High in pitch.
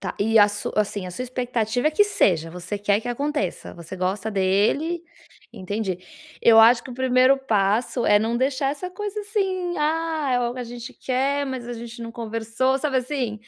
Yes: high, 240 Hz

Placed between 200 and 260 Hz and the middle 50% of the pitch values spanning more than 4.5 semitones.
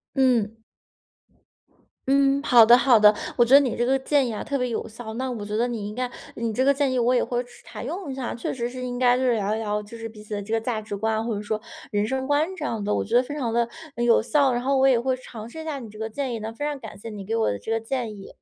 No: high, 235 Hz; average, 3.1 semitones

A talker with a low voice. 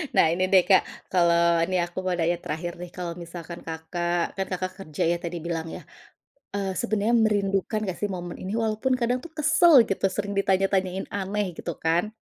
No: medium, 185 Hz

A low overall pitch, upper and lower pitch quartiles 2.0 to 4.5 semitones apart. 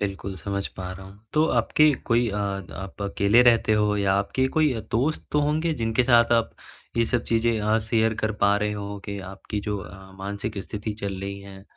Yes: low, 105 Hz; average, 2.8 semitones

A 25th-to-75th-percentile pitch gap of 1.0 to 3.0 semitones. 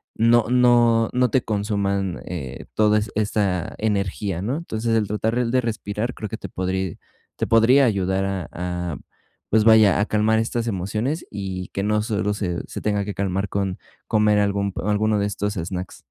Yes: narrow, 2.4 semitones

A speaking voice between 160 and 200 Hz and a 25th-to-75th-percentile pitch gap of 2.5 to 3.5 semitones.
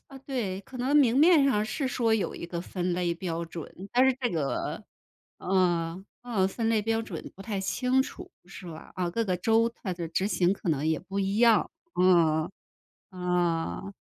No: high, 190 Hz; average, 4.9 semitones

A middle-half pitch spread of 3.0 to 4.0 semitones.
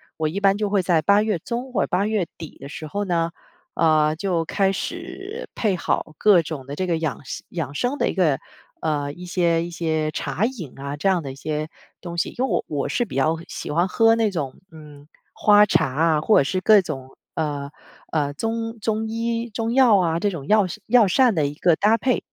No: wide, 5.6 semitones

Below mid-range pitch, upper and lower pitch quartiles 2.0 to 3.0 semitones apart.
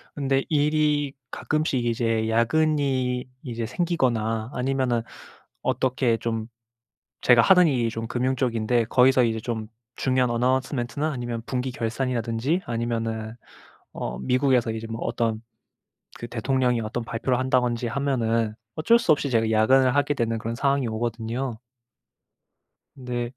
Yes: low, 125 Hz; narrow, 2.6 semitones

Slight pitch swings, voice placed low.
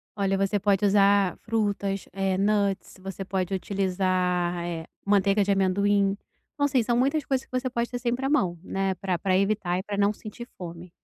No: narrow, 2.1 semitones; high, 195 Hz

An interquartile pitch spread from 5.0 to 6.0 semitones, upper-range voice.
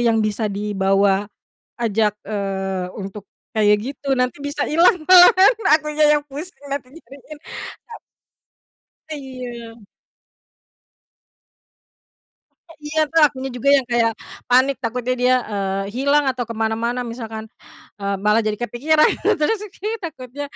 Yes: wide, 5.5 semitones; high, 245 Hz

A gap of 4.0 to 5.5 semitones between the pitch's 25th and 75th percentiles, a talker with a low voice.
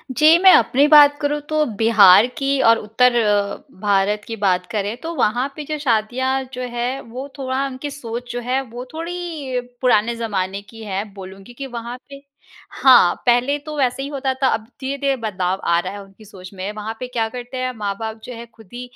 No: average, 4.4 semitones; high, 240 Hz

